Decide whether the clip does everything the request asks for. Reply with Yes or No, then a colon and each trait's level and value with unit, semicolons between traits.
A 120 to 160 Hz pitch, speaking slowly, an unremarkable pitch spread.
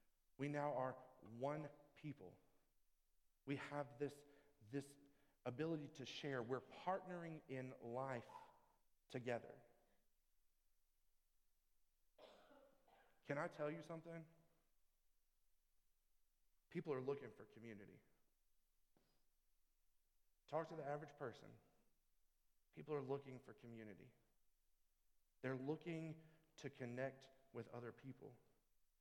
Yes: medium, 140 Hz; slow, 90 wpm; average, 3.4 semitones